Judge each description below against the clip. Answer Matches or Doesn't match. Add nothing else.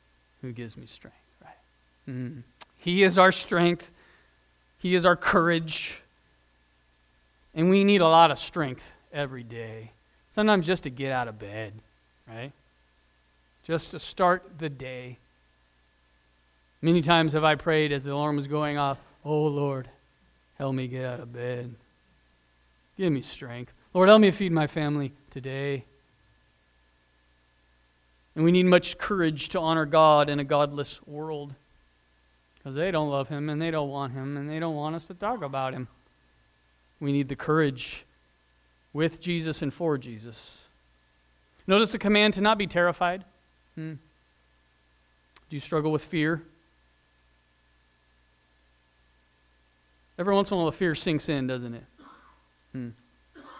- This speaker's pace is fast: Doesn't match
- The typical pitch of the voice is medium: Doesn't match